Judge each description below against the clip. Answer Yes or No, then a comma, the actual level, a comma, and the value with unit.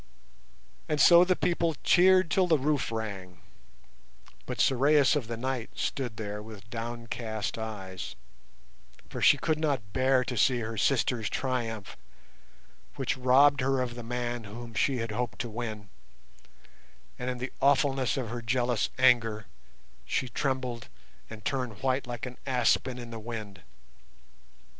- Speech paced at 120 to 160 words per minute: Yes, average, 145 wpm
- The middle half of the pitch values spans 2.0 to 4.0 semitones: Yes, average, 3.1 semitones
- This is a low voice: Yes, low, 120 Hz